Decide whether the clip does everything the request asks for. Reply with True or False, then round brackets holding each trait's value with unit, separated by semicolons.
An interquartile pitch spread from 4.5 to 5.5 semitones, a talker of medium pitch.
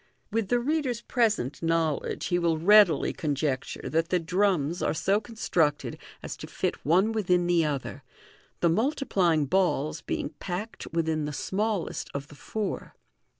True (5.1 semitones; 175 Hz)